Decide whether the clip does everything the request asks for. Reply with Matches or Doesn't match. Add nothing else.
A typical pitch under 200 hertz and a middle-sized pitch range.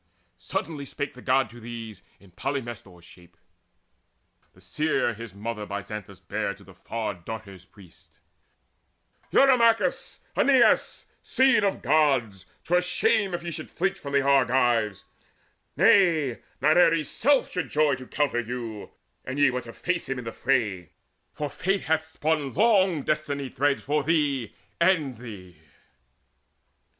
Doesn't match